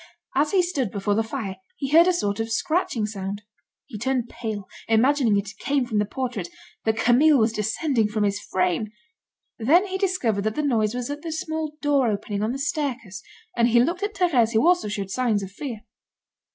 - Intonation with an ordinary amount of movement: No, wide, 5.7 semitones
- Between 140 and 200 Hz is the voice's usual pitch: No, high, 235 Hz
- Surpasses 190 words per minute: Yes, average, 200 wpm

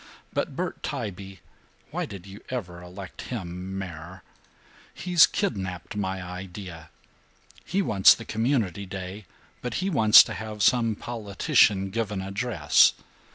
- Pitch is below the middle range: Yes, low, 100 Hz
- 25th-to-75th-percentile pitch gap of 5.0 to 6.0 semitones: No, average, 3.4 semitones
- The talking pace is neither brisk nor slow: No, slow, 130 wpm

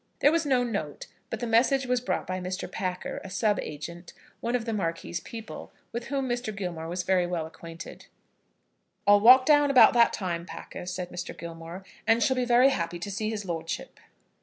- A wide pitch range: Yes, wide, 5.7 semitones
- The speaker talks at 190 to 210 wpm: Yes, average, 195 wpm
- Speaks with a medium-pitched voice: No, high, 200 Hz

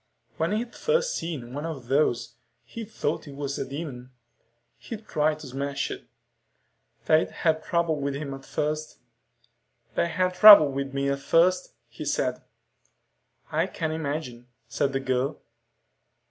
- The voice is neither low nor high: Yes, medium, 150 Hz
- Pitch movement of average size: Yes, average, 3.4 semitones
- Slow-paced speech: No, average, 145 wpm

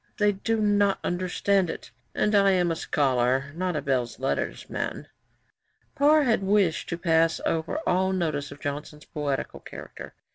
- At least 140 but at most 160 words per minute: Yes, average, 155 wpm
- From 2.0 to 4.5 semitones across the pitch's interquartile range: No, average, 5.3 semitones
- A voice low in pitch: No, medium, 175 Hz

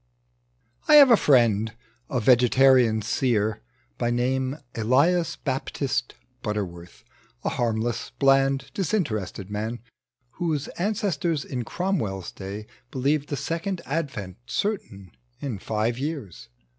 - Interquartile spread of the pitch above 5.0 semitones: Yes, wide, 5.6 semitones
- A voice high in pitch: No, low, 130 Hz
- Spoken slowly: Yes, slow, 105 wpm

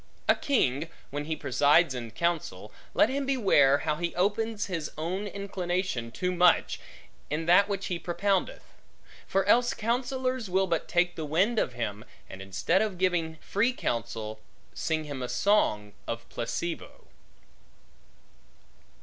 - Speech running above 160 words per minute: No, average, 140 wpm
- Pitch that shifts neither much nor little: No, wide, 5.9 semitones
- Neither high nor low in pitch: Yes, medium, 175 Hz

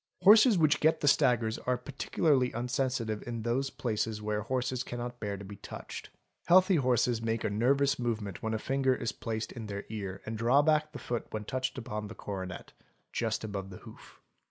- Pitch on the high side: No, low, 120 Hz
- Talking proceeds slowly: No, average, 190 wpm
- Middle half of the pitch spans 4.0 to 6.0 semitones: No, average, 3.6 semitones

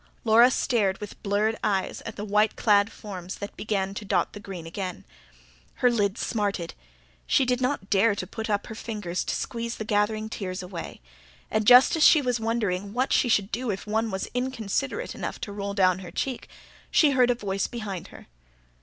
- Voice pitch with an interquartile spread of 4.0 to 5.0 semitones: No, average, 3.0 semitones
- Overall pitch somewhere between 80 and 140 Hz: No, high, 210 Hz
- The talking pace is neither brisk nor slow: Yes, average, 195 wpm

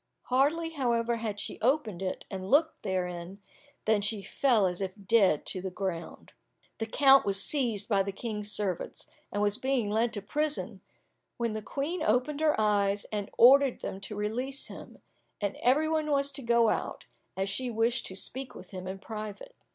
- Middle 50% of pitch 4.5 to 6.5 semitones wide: Yes, average, 5.1 semitones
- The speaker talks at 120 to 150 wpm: No, average, 180 wpm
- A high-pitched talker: Yes, high, 220 Hz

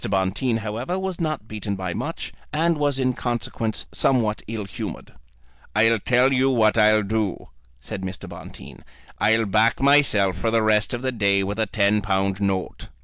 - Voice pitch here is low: Yes, low, 110 Hz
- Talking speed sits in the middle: Yes, average, 170 wpm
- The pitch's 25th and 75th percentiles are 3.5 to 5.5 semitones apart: Yes, average, 4.0 semitones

